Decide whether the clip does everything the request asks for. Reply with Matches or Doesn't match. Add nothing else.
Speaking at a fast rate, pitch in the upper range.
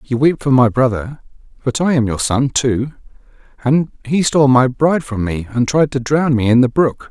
Doesn't match